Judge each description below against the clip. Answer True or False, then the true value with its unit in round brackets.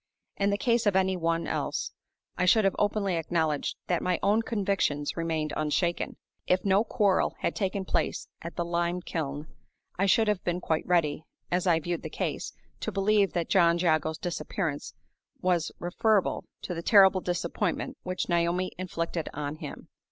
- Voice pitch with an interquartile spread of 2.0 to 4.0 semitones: True (2.7 semitones)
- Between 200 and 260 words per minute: False (170 wpm)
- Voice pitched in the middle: True (175 Hz)